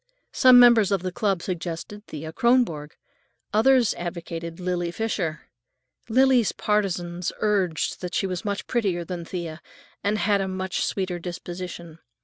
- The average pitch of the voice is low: No, medium, 185 Hz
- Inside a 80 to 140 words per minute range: Yes, slow, 135 wpm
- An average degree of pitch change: Yes, average, 3.5 semitones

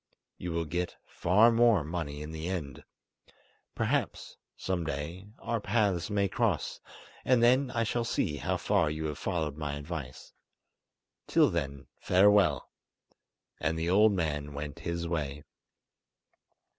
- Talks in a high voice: No, very low, 85 Hz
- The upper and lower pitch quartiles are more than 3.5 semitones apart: Yes, average, 5.2 semitones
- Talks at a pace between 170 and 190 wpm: No, slow, 135 wpm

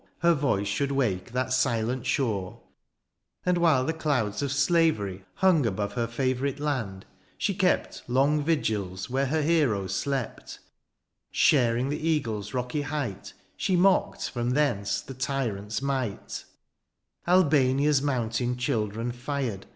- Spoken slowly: Yes, slow, 130 wpm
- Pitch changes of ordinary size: Yes, average, 4.6 semitones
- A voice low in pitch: Yes, low, 130 Hz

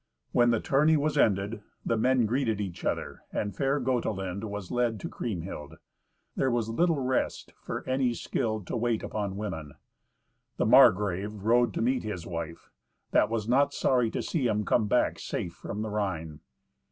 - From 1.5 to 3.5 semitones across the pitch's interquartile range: No, average, 3.9 semitones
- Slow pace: No, average, 170 wpm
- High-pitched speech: No, low, 110 Hz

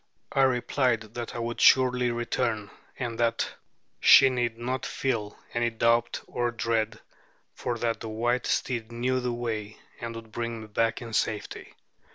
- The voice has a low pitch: Yes, low, 120 Hz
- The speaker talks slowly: No, average, 160 wpm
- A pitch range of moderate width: No, narrow, 1.4 semitones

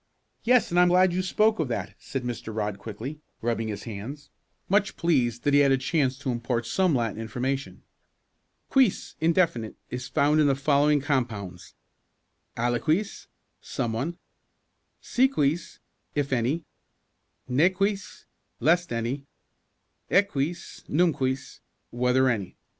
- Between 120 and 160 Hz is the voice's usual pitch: Yes, medium, 140 Hz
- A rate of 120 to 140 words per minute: Yes, slow, 135 wpm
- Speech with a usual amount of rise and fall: No, wide, 6.1 semitones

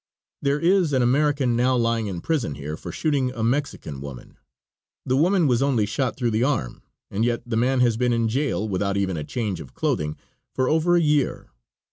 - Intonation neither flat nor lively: Yes, average, 4.9 semitones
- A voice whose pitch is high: No, low, 125 Hz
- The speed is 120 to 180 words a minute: No, average, 200 wpm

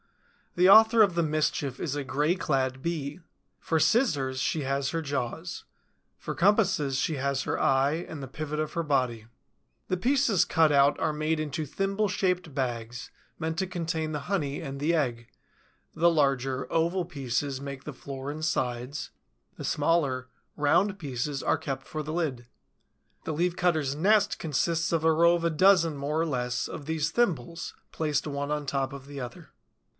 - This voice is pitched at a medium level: Yes, medium, 150 Hz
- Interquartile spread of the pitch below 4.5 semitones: Yes, average, 3.6 semitones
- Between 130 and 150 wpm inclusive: No, average, 175 wpm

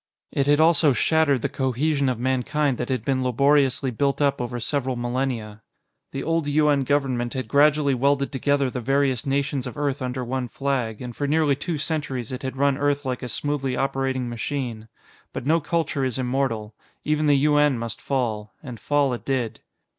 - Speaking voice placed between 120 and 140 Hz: Yes, low, 135 Hz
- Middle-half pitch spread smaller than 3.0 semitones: Yes, narrow, 2.5 semitones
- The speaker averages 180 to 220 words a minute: Yes, average, 185 wpm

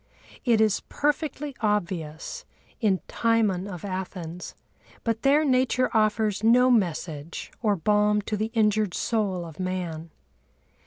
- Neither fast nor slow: No, slow, 115 wpm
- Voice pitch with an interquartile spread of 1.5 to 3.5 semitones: No, average, 3.9 semitones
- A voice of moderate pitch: No, high, 210 Hz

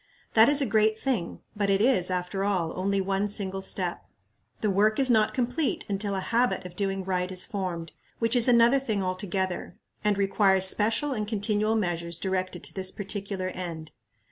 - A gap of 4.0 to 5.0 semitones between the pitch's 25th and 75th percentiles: No, average, 2.7 semitones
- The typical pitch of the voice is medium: No, high, 200 Hz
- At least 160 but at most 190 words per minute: Yes, average, 180 wpm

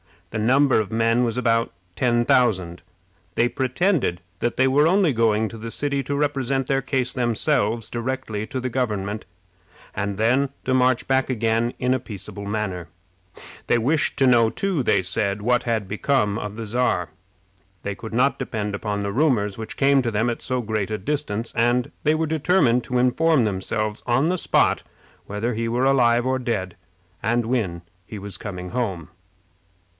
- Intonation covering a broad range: No, average, 3.7 semitones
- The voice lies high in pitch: No, low, 120 Hz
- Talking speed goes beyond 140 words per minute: Yes, average, 175 wpm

